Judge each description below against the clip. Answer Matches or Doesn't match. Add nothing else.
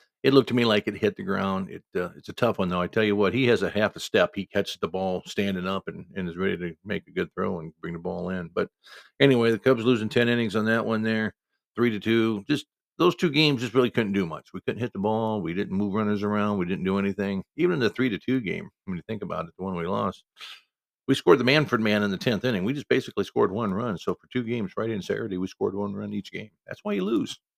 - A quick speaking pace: Matches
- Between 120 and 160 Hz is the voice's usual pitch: Doesn't match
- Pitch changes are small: Doesn't match